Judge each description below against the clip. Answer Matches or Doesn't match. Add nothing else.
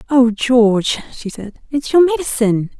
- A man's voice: Doesn't match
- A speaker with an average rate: Matches